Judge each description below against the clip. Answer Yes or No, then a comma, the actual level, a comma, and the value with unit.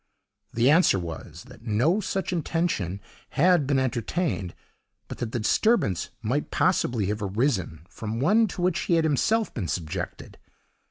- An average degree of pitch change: No, wide, 9.0 semitones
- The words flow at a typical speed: Yes, average, 150 wpm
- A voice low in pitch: Yes, low, 130 Hz